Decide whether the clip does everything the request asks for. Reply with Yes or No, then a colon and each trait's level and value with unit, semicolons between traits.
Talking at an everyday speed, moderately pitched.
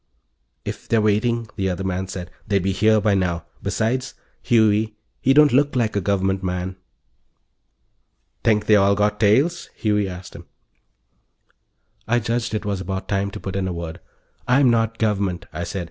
No: average, 170 wpm; low, 105 Hz